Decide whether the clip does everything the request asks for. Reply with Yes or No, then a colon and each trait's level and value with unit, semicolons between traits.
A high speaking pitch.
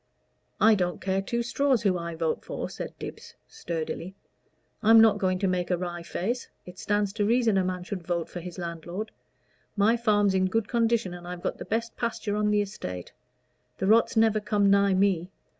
Yes: high, 195 Hz